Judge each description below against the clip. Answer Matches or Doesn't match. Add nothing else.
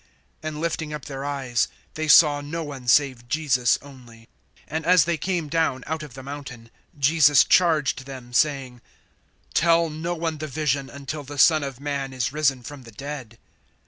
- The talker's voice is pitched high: Doesn't match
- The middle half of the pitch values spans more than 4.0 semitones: Doesn't match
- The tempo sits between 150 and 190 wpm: Matches